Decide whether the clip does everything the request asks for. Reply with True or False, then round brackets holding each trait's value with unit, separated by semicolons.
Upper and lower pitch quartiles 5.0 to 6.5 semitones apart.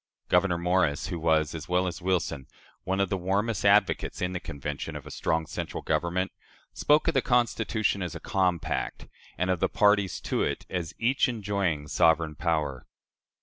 False (3.6 semitones)